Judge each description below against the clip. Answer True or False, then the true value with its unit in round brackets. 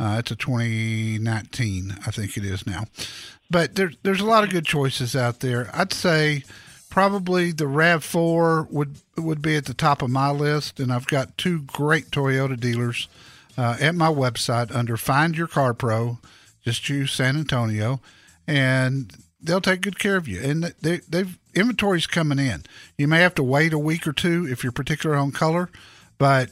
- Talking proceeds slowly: False (185 wpm)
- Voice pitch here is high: False (140 Hz)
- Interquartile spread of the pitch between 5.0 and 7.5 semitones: True (5.3 semitones)